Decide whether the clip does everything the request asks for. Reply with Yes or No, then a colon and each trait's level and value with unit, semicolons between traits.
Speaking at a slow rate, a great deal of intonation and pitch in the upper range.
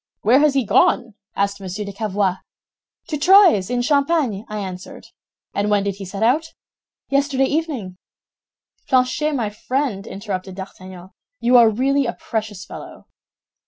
No: average, 145 wpm; wide, 5.8 semitones; high, 220 Hz